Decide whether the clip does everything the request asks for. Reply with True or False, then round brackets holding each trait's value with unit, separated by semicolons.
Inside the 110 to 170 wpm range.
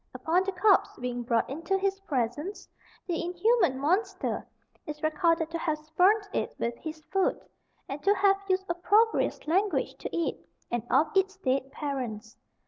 True (155 wpm)